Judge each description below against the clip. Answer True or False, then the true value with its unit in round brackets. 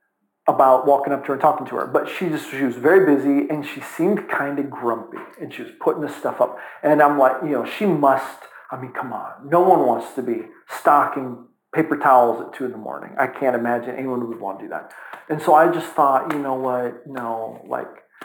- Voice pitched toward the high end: False (135 Hz)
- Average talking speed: False (235 wpm)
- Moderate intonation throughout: True (3.0 semitones)